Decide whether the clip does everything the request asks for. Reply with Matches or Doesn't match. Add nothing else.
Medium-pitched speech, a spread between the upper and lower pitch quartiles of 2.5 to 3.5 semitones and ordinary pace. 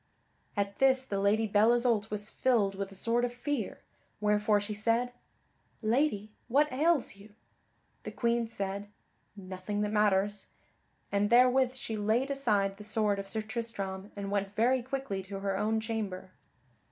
Doesn't match